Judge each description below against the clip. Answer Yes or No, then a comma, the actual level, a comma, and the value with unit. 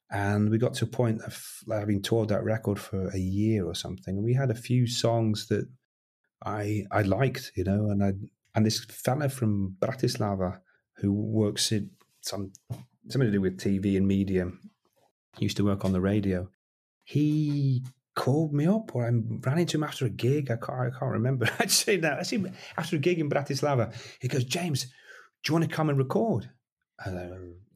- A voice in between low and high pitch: No, low, 110 Hz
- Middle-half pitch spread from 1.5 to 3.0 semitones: No, average, 4.6 semitones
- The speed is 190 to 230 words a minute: Yes, average, 195 wpm